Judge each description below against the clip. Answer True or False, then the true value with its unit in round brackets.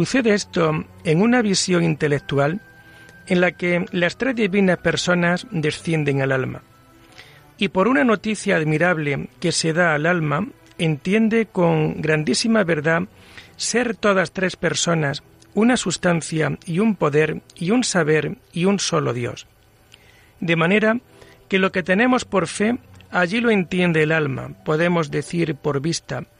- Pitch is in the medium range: True (170 Hz)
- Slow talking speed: False (145 wpm)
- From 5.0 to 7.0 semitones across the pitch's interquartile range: False (4.3 semitones)